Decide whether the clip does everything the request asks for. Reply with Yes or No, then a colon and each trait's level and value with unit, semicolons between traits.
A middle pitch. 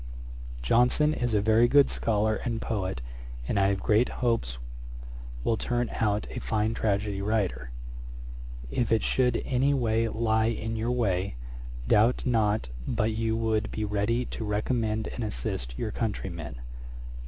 No: low, 110 Hz